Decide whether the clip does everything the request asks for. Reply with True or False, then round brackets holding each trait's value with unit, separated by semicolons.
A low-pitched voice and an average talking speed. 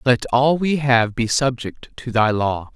True (120 Hz; 195 wpm)